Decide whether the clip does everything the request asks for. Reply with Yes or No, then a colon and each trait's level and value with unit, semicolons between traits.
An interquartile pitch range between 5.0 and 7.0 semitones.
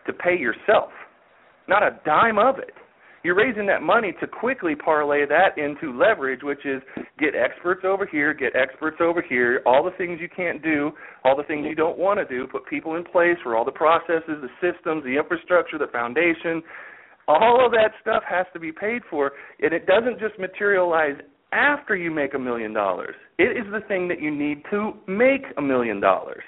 Yes: wide, 5.4 semitones